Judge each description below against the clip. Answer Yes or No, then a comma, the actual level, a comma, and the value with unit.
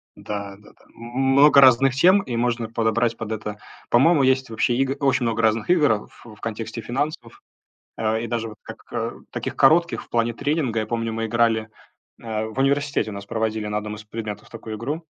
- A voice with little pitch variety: No, average, 3.2 semitones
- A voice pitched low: Yes, low, 115 Hz